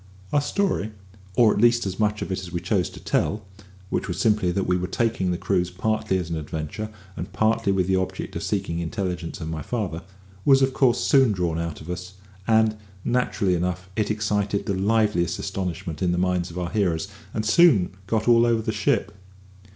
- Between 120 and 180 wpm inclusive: No, fast, 205 wpm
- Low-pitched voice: Yes, very low, 95 Hz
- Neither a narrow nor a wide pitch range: Yes, average, 3.6 semitones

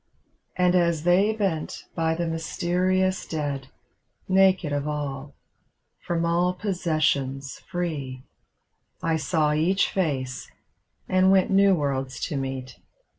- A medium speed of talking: No, slow, 120 wpm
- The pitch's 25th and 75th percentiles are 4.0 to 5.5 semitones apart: Yes, average, 4.4 semitones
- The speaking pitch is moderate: Yes, medium, 165 Hz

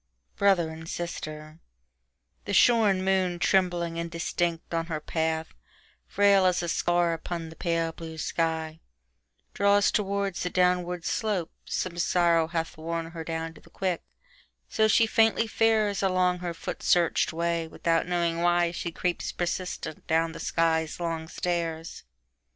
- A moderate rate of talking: No, slow, 130 wpm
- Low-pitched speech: No, medium, 170 Hz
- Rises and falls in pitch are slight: Yes, narrow, 2.0 semitones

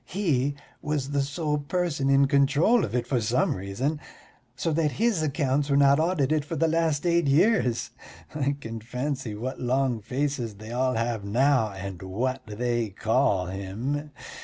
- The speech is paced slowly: No, average, 160 wpm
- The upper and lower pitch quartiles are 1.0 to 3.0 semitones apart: No, average, 4.3 semitones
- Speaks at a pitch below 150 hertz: Yes, low, 135 Hz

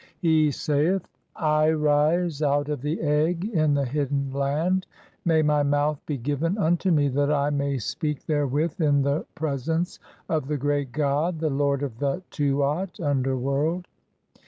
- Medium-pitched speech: Yes, medium, 150 Hz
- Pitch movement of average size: No, narrow, 2.1 semitones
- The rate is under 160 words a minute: No, average, 175 wpm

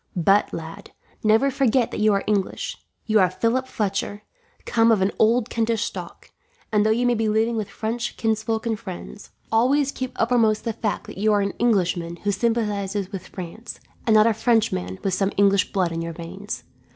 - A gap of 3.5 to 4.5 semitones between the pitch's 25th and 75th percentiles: No, average, 2.7 semitones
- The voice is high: Yes, high, 215 Hz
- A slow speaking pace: No, average, 190 wpm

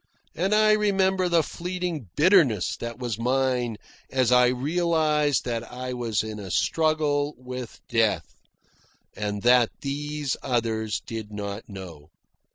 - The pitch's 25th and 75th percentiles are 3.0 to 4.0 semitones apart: No, wide, 5.5 semitones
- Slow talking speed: Yes, slow, 130 wpm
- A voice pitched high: No, low, 125 Hz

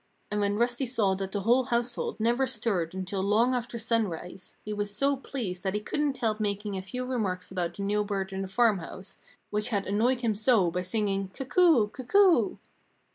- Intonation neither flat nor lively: Yes, average, 4.0 semitones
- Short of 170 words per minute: No, average, 190 wpm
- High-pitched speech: Yes, high, 210 Hz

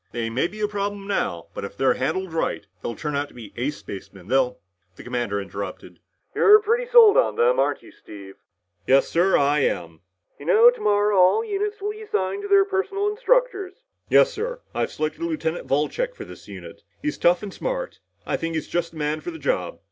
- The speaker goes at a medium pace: No, fast, 215 wpm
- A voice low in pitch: No, high, 195 Hz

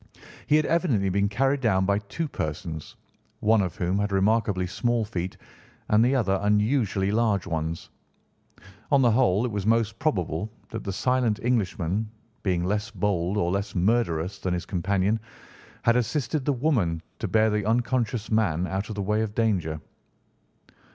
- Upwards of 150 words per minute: Yes, average, 165 wpm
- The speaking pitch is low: Yes, low, 105 Hz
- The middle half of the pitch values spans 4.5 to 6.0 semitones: No, average, 3.8 semitones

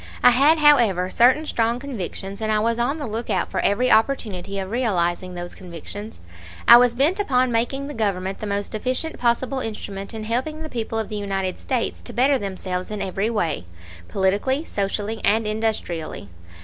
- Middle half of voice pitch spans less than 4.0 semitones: No, average, 4.3 semitones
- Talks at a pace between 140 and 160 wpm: No, average, 175 wpm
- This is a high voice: Yes, high, 220 Hz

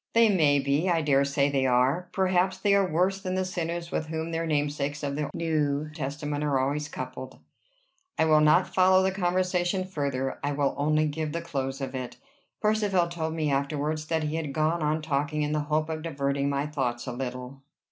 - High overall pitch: No, medium, 155 Hz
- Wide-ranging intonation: No, average, 3.4 semitones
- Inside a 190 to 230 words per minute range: Yes, average, 200 wpm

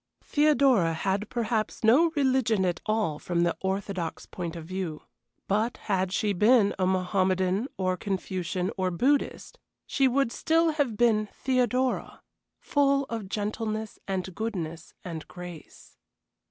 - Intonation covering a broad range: No, average, 4.8 semitones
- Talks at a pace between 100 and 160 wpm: Yes, average, 140 wpm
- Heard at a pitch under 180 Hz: No, high, 205 Hz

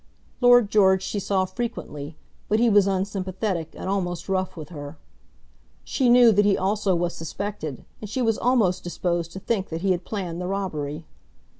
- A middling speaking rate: Yes, average, 175 wpm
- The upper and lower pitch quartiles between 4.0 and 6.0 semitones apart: No, average, 3.2 semitones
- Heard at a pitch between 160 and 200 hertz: Yes, high, 190 Hz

